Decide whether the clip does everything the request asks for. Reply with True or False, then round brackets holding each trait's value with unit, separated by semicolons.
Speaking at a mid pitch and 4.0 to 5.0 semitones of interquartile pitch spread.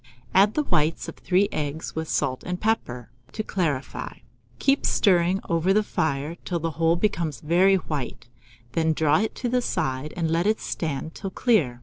True (165 Hz; 4.4 semitones)